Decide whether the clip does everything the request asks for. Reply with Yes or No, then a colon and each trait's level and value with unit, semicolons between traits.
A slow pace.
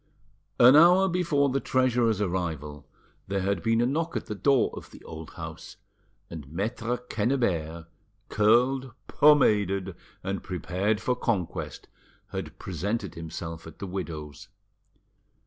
Yes: slow, 130 wpm